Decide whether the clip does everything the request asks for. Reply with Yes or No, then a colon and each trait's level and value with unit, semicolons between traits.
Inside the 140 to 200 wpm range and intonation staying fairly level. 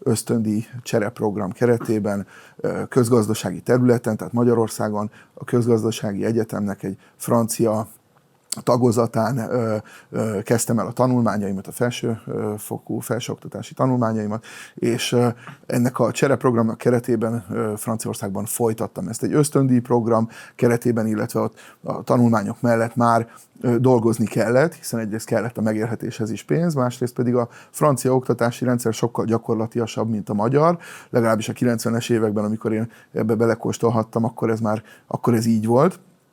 No: average, 130 wpm; narrow, 1.8 semitones